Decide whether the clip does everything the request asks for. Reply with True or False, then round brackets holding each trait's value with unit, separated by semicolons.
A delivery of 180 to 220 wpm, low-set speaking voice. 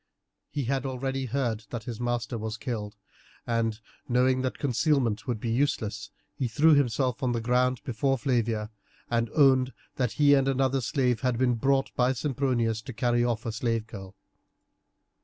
False (165 wpm; 125 Hz)